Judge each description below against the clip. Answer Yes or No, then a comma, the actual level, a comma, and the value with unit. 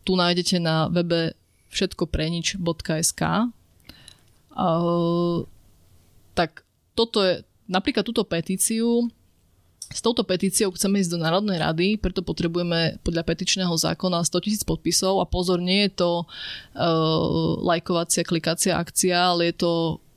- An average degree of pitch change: No, narrow, 2.3 semitones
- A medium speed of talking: Yes, average, 120 wpm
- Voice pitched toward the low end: No, medium, 175 Hz